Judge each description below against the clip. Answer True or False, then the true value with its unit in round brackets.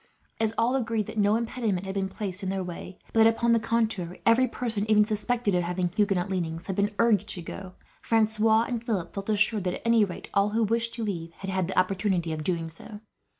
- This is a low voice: False (205 Hz)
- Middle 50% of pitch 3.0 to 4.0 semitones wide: True (3.5 semitones)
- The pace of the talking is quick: True (230 wpm)